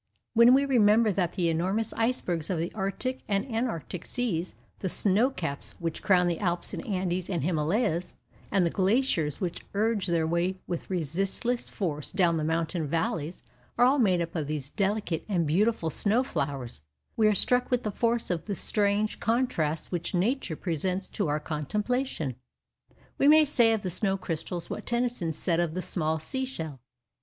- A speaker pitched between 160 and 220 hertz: Yes, medium, 185 Hz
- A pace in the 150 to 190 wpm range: Yes, average, 175 wpm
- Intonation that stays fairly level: No, average, 5.2 semitones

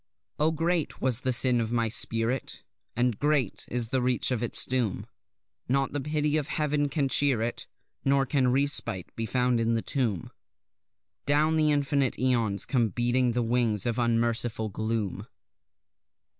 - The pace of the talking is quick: No, average, 155 wpm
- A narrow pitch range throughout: No, average, 3.4 semitones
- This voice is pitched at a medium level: No, low, 125 Hz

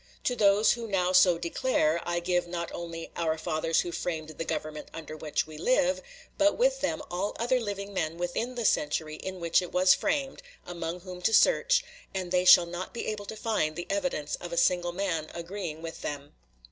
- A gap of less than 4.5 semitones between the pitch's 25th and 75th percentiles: Yes, average, 3.9 semitones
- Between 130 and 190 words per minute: No, average, 200 wpm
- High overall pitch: No, medium, 175 Hz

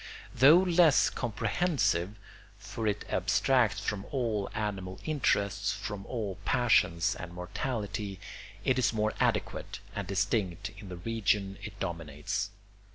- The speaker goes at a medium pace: No, slow, 120 wpm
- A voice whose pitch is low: Yes, low, 105 Hz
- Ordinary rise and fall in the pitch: Yes, average, 3.4 semitones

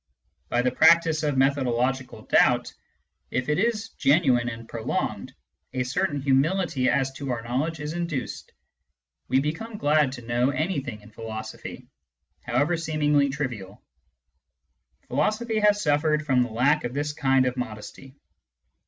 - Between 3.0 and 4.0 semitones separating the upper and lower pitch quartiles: Yes, average, 3.7 semitones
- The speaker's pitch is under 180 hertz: Yes, medium, 140 Hz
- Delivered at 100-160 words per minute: Yes, slow, 135 wpm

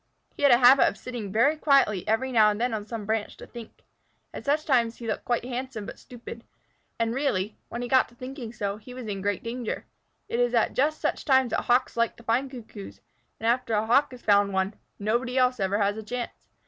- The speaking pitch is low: No, high, 235 Hz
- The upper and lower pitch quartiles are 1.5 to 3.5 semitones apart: Yes, average, 3.0 semitones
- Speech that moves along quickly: Yes, fast, 225 wpm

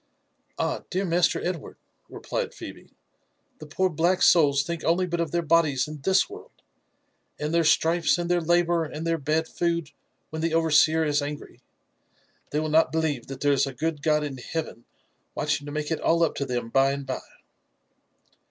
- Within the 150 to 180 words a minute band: No, average, 190 wpm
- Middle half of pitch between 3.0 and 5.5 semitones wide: No, narrow, 2.6 semitones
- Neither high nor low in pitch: Yes, medium, 160 Hz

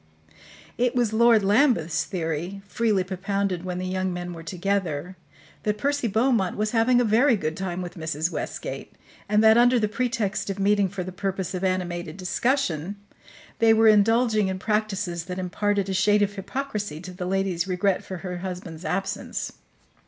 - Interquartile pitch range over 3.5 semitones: No, average, 3.1 semitones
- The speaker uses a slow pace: No, average, 170 wpm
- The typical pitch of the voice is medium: No, high, 195 Hz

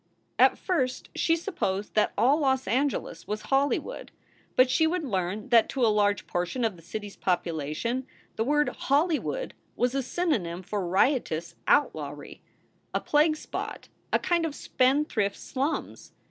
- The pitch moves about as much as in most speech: No, wide, 6.5 semitones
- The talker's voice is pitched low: No, very high, 255 Hz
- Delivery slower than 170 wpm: Yes, average, 150 wpm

